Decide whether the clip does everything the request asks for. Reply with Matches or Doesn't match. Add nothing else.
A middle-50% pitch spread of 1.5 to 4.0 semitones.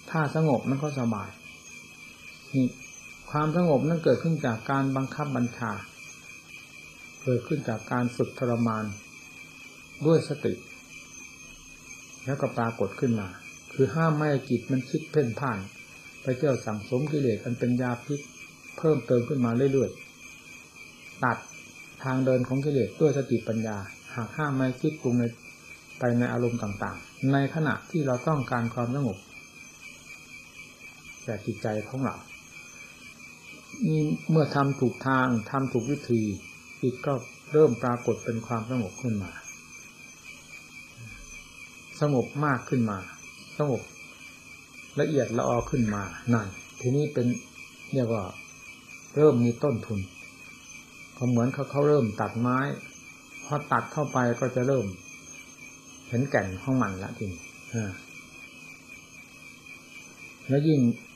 Matches